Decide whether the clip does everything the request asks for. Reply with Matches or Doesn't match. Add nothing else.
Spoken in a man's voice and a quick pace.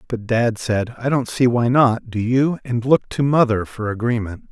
Matches